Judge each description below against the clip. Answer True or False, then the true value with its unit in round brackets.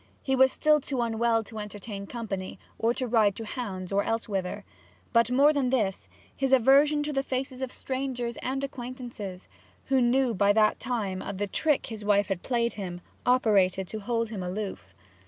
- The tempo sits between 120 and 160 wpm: False (180 wpm)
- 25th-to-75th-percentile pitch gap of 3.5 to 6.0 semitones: True (4.4 semitones)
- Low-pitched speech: False (230 Hz)